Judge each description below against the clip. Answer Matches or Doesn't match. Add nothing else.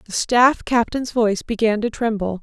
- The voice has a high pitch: Matches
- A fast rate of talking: Doesn't match